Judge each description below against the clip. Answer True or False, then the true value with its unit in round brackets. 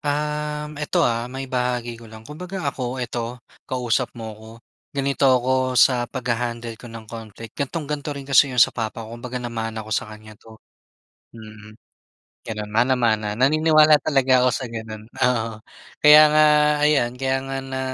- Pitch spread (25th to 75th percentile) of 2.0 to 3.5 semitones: True (3.2 semitones)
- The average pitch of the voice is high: False (125 Hz)